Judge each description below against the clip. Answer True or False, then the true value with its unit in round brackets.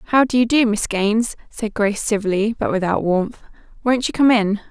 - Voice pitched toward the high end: True (220 Hz)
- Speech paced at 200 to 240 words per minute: True (205 wpm)